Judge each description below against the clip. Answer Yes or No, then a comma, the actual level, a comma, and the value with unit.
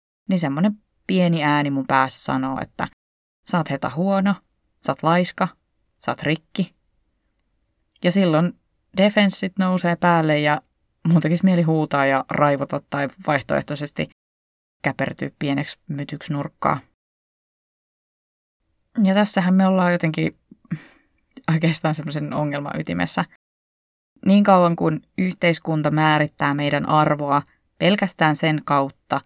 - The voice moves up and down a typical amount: Yes, average, 4.1 semitones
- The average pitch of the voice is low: No, medium, 155 Hz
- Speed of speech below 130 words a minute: Yes, average, 110 wpm